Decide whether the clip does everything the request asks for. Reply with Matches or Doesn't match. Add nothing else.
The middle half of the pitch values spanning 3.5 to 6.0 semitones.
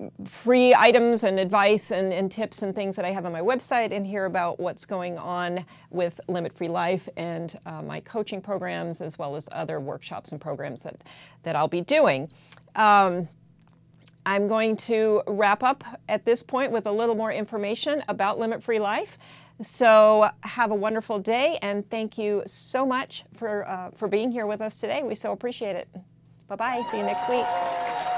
Matches